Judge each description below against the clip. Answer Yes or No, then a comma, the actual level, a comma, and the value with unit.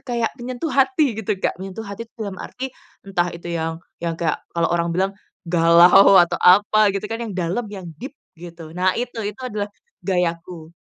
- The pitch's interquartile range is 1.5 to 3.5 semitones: No, average, 4.6 semitones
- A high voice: Yes, high, 195 Hz